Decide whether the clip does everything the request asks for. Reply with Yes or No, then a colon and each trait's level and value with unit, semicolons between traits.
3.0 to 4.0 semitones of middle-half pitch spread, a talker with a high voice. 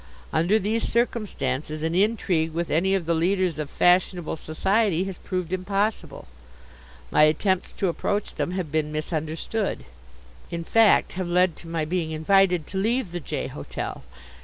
No: average, 3.5 semitones; medium, 180 Hz